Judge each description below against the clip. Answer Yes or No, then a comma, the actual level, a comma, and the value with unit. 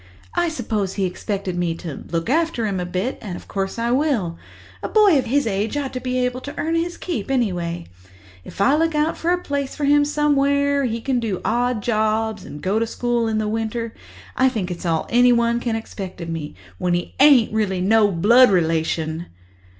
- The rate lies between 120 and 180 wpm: No, fast, 205 wpm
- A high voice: Yes, high, 225 Hz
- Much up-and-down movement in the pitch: Yes, wide, 6.4 semitones